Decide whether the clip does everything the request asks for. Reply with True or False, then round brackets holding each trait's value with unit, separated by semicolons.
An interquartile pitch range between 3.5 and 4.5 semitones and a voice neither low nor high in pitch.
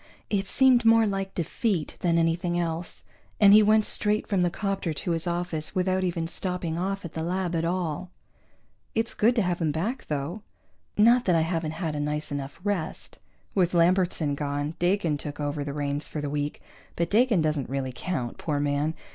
True (4.2 semitones; 170 Hz)